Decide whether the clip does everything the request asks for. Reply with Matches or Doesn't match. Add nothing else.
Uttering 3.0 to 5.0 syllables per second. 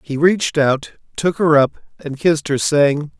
Matches